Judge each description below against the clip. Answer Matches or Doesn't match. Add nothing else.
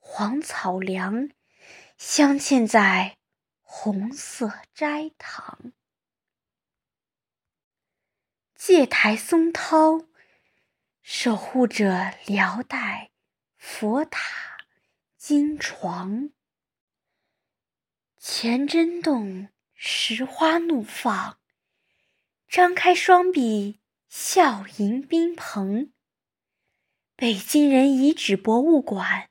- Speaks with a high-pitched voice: Matches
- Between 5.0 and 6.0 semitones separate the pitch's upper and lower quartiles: Doesn't match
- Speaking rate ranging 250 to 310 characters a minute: Doesn't match